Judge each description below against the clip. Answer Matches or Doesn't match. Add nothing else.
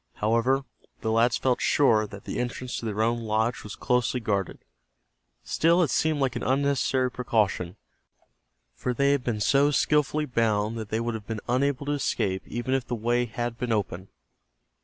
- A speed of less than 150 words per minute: Doesn't match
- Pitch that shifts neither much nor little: Matches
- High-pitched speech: Doesn't match